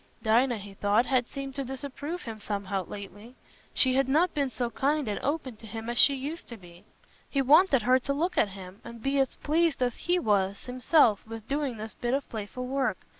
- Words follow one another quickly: Yes, fast, 215 wpm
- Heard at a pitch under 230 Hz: No, very high, 250 Hz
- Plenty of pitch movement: No, average, 4.4 semitones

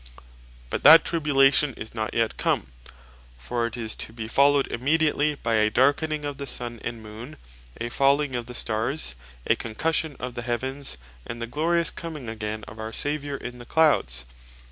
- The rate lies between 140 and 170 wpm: No, average, 185 wpm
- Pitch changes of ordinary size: Yes, average, 4.3 semitones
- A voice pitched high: No, low, 125 Hz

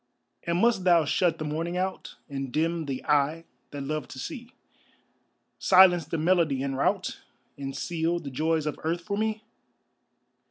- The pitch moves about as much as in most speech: Yes, average, 3.6 semitones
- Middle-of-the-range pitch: Yes, medium, 165 Hz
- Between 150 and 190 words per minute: Yes, average, 160 wpm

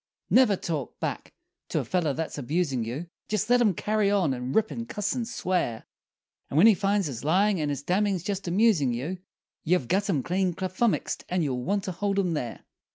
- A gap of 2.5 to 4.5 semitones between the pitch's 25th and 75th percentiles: No, wide, 5.4 semitones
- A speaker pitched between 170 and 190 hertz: Yes, medium, 185 Hz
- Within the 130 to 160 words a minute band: No, fast, 205 wpm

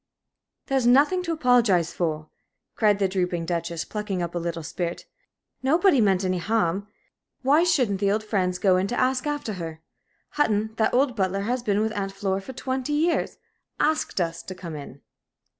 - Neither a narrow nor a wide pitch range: No, wide, 6.0 semitones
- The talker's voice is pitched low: No, high, 205 Hz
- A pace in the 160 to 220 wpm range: Yes, average, 180 wpm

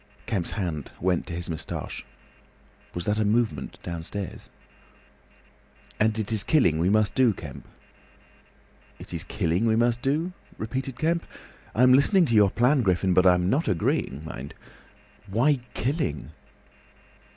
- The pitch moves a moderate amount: No, wide, 6.2 semitones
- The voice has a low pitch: Yes, low, 105 Hz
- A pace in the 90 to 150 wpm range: Yes, average, 140 wpm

